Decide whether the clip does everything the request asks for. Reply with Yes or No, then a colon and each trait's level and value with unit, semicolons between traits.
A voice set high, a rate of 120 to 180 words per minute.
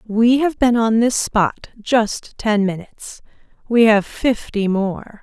Yes: high, 220 Hz; average, 150 wpm